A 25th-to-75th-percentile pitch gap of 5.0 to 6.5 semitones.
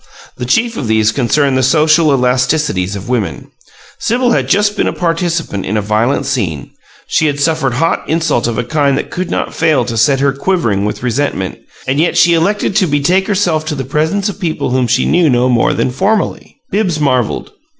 Yes: wide, 5.4 semitones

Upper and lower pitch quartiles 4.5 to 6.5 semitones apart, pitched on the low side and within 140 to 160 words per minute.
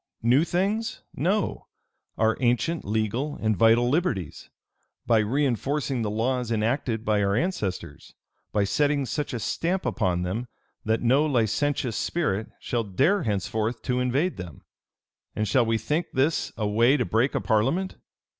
Yes: average, 5.0 semitones; low, 120 Hz; average, 145 wpm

